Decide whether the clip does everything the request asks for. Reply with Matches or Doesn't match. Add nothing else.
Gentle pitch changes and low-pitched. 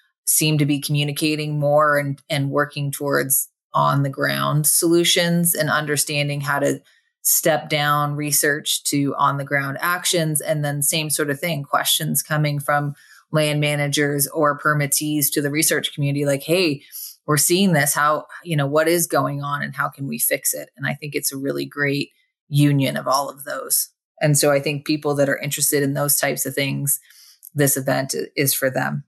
Doesn't match